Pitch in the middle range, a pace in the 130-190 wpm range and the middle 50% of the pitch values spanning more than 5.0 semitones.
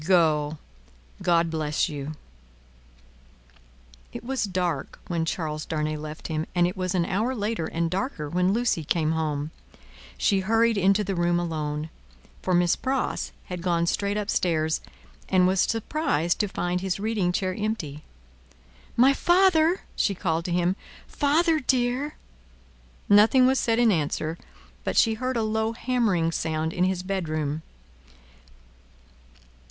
Yes: medium, 180 Hz; average, 140 wpm; wide, 5.5 semitones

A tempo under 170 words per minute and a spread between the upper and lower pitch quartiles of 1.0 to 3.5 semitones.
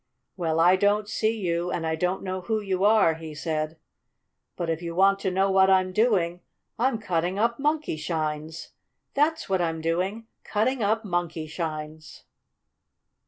No: average, 155 wpm; average, 4.3 semitones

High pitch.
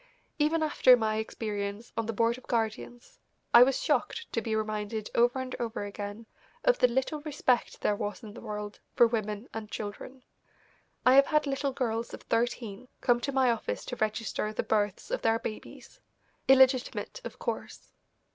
Yes: high, 230 Hz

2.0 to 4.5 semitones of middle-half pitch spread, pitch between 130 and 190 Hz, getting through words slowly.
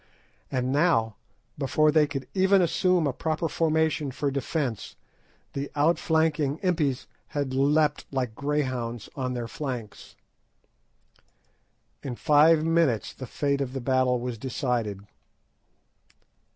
Yes: average, 3.7 semitones; medium, 140 Hz; slow, 115 wpm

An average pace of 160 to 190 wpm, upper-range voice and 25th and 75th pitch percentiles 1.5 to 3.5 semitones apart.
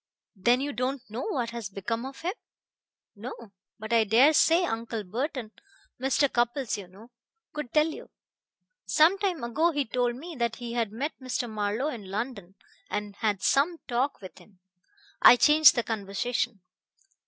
No: average, 165 wpm; high, 240 Hz; average, 4.5 semitones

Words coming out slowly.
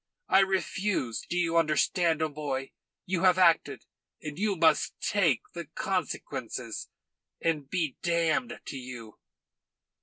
Yes: slow, 120 wpm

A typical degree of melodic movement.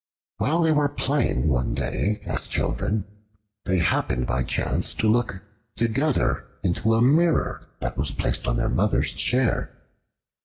No: wide, 8.5 semitones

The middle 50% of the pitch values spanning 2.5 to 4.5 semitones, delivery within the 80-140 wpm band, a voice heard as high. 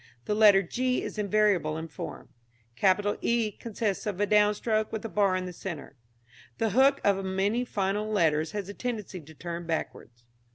No: average, 3.0 semitones; average, 170 wpm; high, 205 Hz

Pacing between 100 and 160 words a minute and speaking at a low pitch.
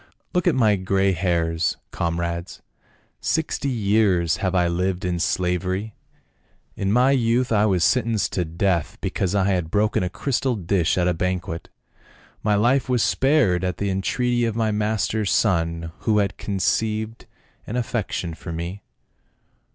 Yes: average, 155 wpm; very low, 95 Hz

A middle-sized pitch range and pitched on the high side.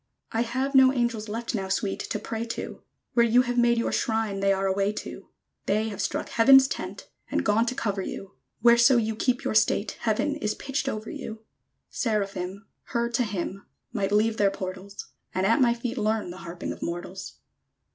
Yes: average, 3.2 semitones; high, 220 Hz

